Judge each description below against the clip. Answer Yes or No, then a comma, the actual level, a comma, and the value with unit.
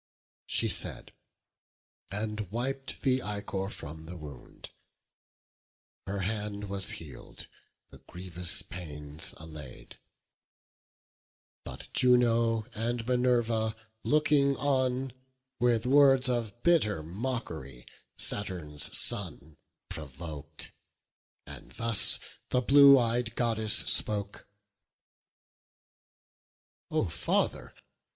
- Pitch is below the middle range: Yes, low, 110 Hz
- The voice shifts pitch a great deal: Yes, wide, 6.1 semitones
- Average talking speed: No, slow, 85 wpm